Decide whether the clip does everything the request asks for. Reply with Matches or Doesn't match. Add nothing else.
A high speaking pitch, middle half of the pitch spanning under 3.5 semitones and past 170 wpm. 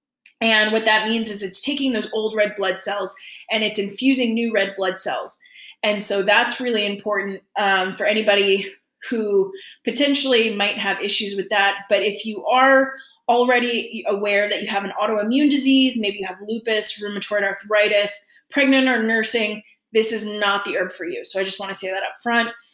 Matches